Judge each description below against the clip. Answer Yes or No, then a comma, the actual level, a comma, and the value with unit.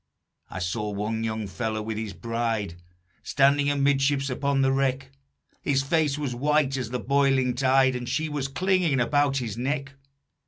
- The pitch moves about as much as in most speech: Yes, average, 3.6 semitones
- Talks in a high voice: No, low, 135 Hz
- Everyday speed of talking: Yes, average, 160 wpm